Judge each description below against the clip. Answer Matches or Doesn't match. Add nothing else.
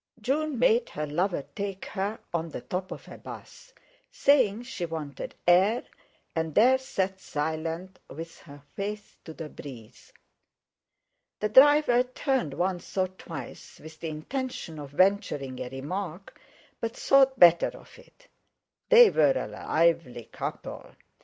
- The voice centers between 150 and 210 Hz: Matches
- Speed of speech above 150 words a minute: Doesn't match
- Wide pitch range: Matches